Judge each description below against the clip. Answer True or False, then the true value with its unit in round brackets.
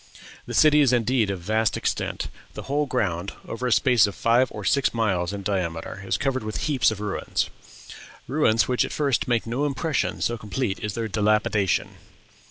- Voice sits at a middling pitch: False (115 Hz)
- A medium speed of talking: True (180 wpm)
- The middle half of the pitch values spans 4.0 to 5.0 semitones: True (4.3 semitones)